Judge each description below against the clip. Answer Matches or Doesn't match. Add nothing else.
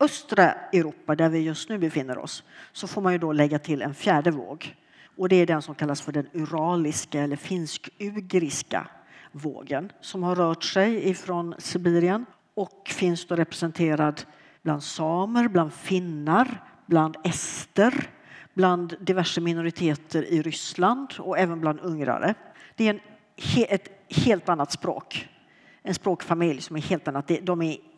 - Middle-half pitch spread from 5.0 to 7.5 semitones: Doesn't match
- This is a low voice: Doesn't match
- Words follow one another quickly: Doesn't match